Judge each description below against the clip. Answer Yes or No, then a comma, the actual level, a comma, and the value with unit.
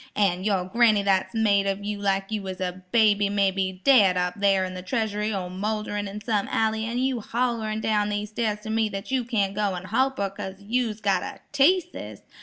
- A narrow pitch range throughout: Yes, narrow, 2.2 semitones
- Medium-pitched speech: No, high, 205 Hz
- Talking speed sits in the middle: No, fast, 215 wpm